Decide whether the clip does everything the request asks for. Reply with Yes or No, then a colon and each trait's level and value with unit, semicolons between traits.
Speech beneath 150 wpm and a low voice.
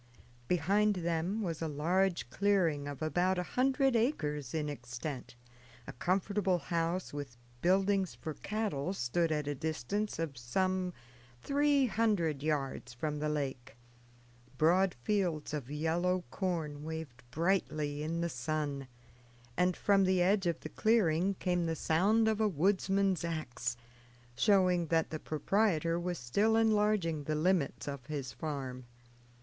No: average, 140 wpm; medium, 170 Hz